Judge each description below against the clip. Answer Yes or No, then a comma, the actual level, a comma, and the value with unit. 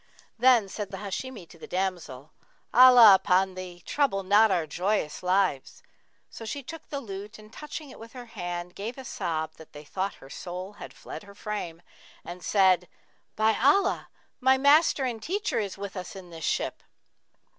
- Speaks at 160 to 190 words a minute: Yes, average, 175 wpm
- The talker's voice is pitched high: Yes, high, 200 Hz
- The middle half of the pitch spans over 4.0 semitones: Yes, average, 5.0 semitones